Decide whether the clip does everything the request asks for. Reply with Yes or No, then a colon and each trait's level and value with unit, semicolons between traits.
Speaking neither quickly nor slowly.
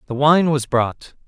Yes: average, 190 wpm